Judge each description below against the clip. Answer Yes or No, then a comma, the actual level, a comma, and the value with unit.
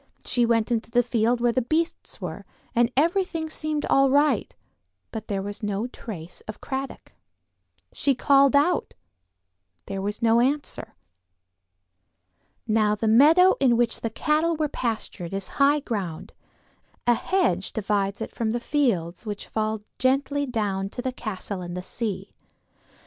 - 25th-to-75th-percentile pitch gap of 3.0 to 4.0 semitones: No, average, 5.1 semitones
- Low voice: No, high, 235 Hz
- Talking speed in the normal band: Yes, average, 150 wpm